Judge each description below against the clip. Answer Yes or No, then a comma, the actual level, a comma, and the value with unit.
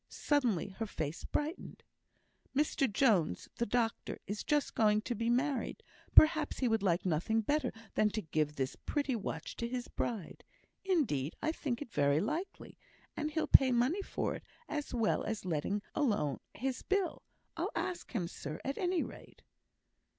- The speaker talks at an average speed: Yes, average, 165 wpm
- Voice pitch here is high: Yes, high, 235 Hz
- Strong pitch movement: Yes, wide, 7.5 semitones